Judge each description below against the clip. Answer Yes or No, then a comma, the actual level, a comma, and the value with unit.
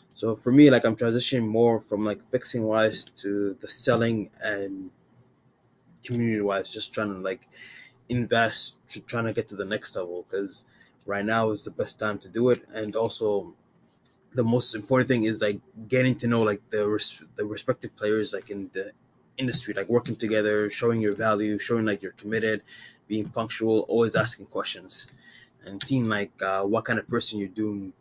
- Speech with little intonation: Yes, narrow, 2.3 semitones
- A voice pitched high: No, low, 110 Hz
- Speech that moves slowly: No, average, 185 wpm